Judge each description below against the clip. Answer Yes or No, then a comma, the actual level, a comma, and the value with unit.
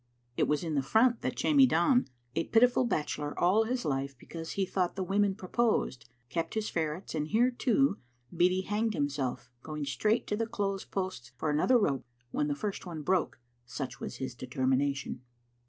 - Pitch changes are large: Yes, wide, 7.0 semitones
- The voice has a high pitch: No, medium, 175 Hz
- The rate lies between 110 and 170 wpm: No, average, 180 wpm